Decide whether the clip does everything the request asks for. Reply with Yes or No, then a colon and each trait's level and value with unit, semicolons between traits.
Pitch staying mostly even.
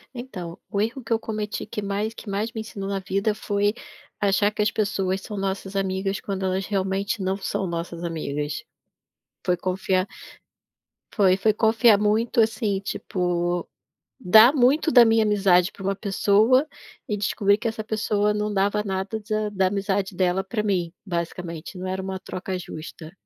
Yes: narrow, 2.3 semitones